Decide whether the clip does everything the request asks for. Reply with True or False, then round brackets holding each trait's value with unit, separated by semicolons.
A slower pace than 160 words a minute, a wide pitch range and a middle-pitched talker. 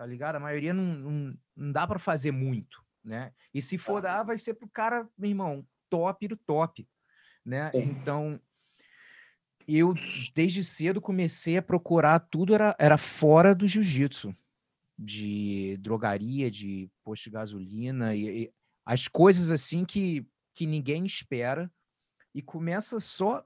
True (150 wpm; 6.6 semitones; 155 Hz)